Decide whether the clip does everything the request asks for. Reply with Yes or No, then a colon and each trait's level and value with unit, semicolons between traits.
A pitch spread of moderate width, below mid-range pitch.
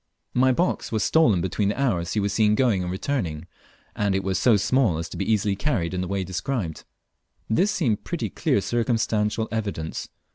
Yes: average, 4.2 semitones; low, 105 Hz